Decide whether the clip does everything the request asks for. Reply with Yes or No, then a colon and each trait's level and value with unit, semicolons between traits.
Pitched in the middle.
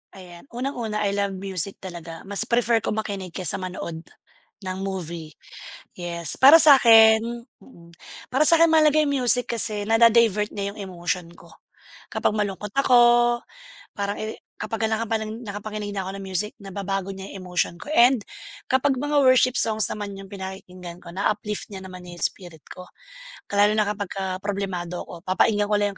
No: high, 205 Hz